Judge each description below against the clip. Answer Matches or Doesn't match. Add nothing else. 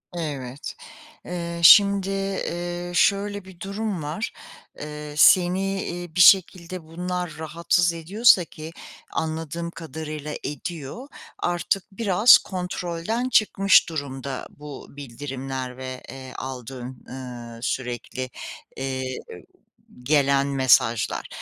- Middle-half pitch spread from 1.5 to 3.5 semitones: Doesn't match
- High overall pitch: Doesn't match